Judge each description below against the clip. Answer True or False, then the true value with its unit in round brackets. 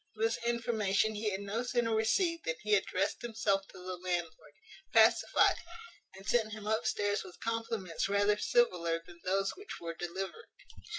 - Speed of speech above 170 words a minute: False (160 wpm)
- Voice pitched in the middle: False (205 Hz)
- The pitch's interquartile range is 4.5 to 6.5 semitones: False (3.5 semitones)